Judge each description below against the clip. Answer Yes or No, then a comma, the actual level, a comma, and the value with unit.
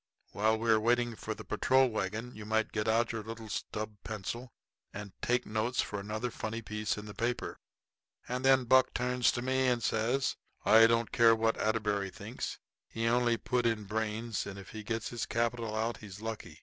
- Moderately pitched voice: No, low, 115 Hz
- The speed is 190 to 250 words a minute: Yes, average, 195 wpm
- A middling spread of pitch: No, narrow, 1.9 semitones